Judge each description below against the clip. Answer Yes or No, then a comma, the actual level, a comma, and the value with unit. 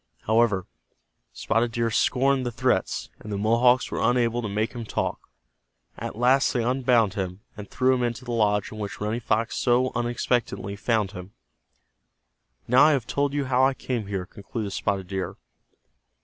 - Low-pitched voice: Yes, low, 115 Hz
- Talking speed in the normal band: Yes, average, 170 wpm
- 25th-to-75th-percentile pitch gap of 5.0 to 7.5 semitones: No, average, 3.3 semitones